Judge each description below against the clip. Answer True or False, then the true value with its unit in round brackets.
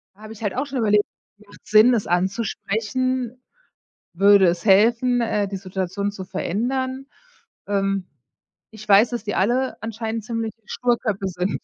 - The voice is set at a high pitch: True (215 Hz)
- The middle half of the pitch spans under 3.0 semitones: False (3.3 semitones)